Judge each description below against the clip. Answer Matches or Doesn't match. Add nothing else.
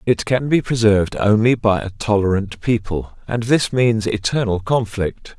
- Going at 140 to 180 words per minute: Matches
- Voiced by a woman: Doesn't match